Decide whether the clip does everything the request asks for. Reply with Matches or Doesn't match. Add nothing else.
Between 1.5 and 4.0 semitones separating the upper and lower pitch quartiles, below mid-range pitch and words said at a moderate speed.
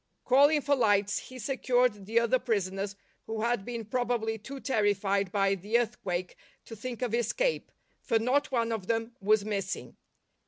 Doesn't match